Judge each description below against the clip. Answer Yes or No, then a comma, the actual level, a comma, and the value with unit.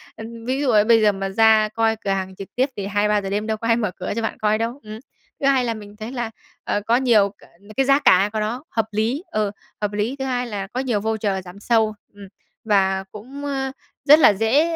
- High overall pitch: Yes, high, 220 Hz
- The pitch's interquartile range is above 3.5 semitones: No, average, 3.1 semitones